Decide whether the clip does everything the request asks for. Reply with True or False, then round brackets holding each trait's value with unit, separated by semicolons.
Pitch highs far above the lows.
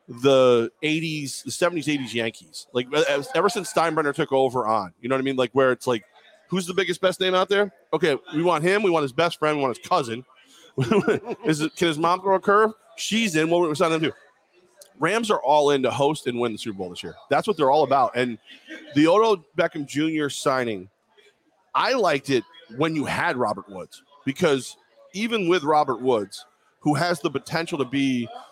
True (5.9 semitones)